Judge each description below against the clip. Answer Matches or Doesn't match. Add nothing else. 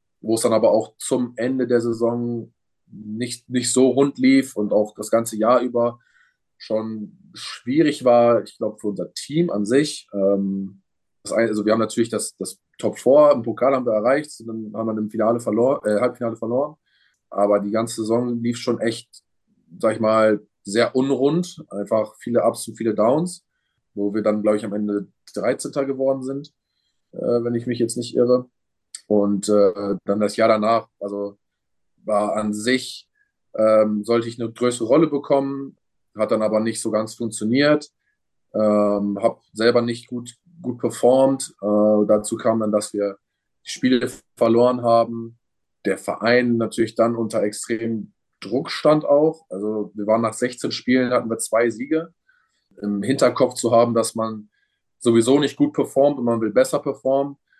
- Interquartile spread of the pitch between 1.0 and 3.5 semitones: Matches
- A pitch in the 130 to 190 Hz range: Doesn't match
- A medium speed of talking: Matches